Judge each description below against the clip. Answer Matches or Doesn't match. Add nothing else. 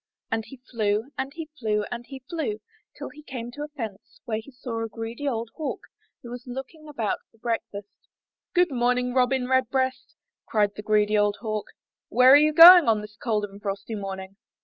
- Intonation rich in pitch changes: Doesn't match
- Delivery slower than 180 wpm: Doesn't match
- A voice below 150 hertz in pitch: Doesn't match